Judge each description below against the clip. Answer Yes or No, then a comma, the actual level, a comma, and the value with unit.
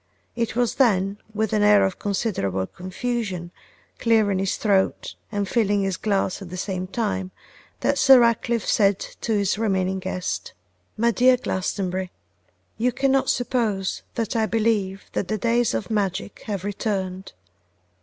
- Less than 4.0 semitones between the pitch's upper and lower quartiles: Yes, average, 3.3 semitones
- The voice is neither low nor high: No, high, 205 Hz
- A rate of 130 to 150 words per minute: Yes, average, 145 wpm